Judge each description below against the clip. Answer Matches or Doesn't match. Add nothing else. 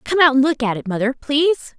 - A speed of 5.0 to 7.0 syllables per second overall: Matches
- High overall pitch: Matches